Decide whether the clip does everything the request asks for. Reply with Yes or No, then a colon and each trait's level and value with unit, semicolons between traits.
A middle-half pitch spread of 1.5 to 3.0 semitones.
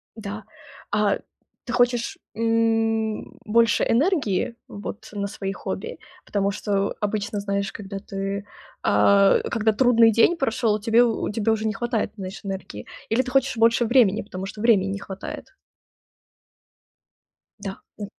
Yes: narrow, 2.4 semitones